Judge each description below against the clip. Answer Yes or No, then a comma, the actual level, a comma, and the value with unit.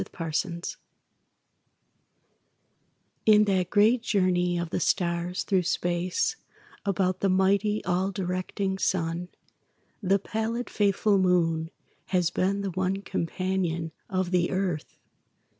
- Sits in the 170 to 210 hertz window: Yes, medium, 185 Hz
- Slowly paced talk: Yes, slow, 115 wpm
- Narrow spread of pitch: Yes, narrow, 2.2 semitones